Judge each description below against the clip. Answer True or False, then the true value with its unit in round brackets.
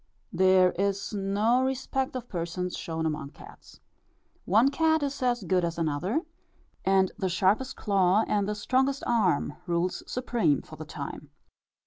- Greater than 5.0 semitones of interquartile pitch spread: True (5.5 semitones)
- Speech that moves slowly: False (145 wpm)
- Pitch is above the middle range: True (195 Hz)